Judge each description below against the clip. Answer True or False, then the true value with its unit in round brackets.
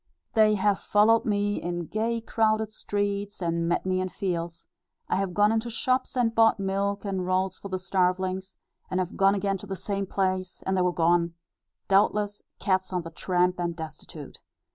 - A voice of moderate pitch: False (195 Hz)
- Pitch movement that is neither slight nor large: False (2.2 semitones)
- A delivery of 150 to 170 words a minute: False (185 wpm)